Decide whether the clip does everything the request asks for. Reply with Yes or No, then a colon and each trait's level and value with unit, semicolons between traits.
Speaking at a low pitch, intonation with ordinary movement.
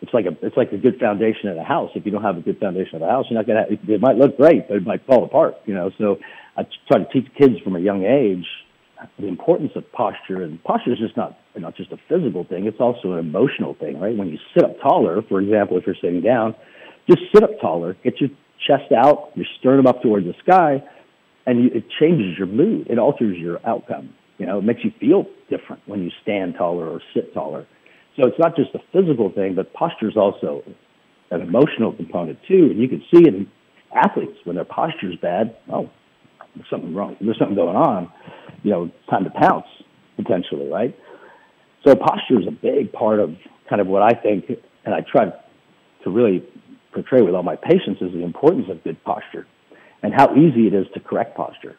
No: low, 115 Hz; wide, 6.8 semitones